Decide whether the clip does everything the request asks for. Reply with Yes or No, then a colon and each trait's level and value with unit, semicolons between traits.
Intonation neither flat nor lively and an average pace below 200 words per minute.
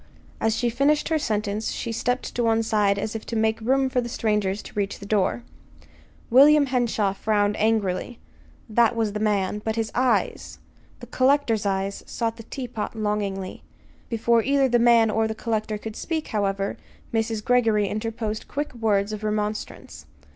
No: narrow, 2.3 semitones; average, 165 wpm